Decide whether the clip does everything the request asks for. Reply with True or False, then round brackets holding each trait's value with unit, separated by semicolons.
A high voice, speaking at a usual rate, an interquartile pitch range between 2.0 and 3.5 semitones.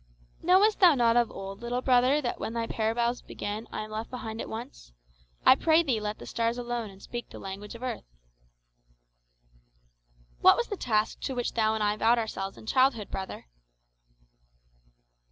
True (230 Hz; 175 wpm; 2.7 semitones)